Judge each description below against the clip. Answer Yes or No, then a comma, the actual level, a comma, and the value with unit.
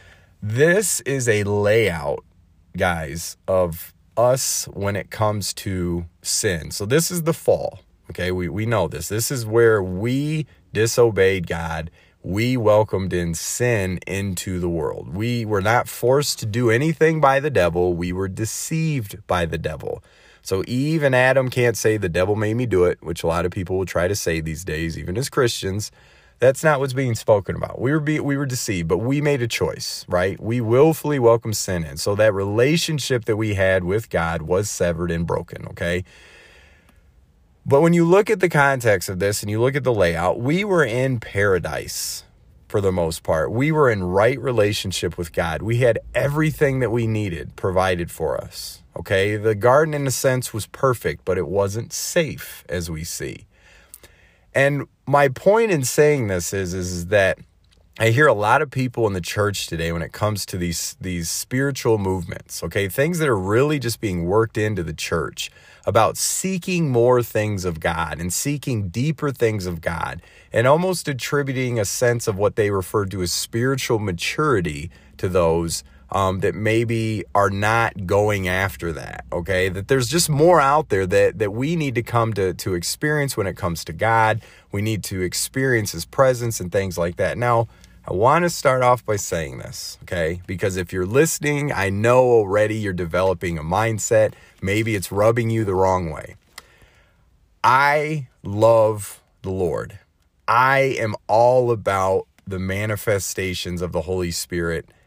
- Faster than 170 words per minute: Yes, average, 180 wpm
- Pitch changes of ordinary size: No, wide, 5.8 semitones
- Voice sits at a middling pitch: No, low, 105 Hz